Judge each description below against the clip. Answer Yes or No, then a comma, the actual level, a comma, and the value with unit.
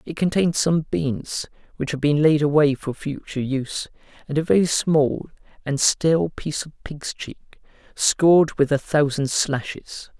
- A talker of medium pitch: Yes, medium, 145 Hz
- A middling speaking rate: Yes, average, 160 wpm